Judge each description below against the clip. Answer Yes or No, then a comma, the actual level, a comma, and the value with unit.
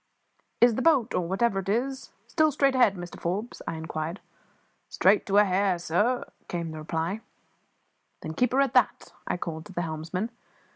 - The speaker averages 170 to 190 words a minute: Yes, average, 180 wpm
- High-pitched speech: Yes, high, 195 Hz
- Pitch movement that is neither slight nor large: No, wide, 6.1 semitones